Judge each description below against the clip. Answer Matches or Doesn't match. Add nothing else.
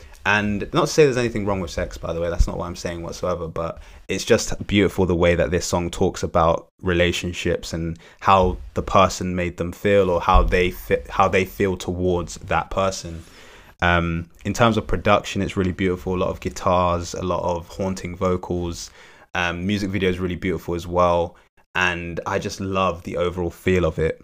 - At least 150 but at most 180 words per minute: Doesn't match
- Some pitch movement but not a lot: Doesn't match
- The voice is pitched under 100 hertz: Matches